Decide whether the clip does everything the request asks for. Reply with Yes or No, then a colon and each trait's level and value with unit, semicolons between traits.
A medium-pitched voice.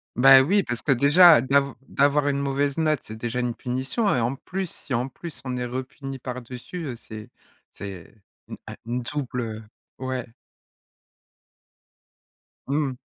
No: low, 130 Hz